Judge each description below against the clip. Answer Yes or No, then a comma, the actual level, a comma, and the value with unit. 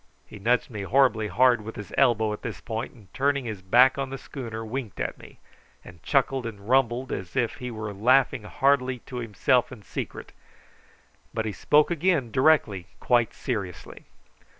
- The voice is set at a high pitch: No, low, 120 Hz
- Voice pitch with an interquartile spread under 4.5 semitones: Yes, average, 3.6 semitones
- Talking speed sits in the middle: Yes, average, 175 wpm